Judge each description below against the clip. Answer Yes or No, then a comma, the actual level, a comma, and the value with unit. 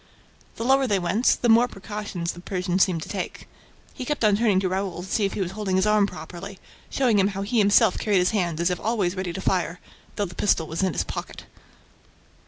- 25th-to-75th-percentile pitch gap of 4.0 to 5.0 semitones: No, average, 2.8 semitones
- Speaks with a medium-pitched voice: No, high, 195 Hz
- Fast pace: Yes, fast, 230 wpm